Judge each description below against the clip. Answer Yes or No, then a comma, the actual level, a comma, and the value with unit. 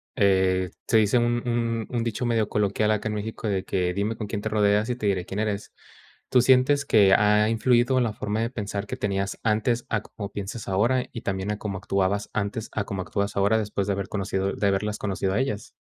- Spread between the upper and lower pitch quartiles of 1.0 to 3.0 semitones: Yes, narrow, 2.4 semitones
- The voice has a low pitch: Yes, low, 105 Hz